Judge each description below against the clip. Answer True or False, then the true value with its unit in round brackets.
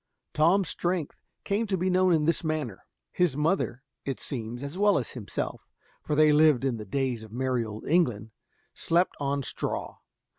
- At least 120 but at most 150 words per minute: False (175 wpm)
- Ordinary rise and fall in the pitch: False (6.0 semitones)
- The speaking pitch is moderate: True (150 Hz)